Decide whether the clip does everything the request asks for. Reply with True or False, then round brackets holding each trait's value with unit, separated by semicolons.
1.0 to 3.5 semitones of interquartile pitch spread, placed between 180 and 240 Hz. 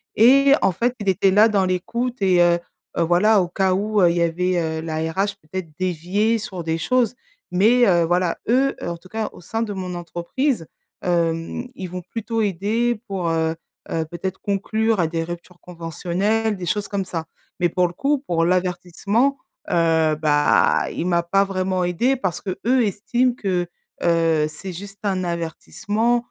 False (4.0 semitones; 185 Hz)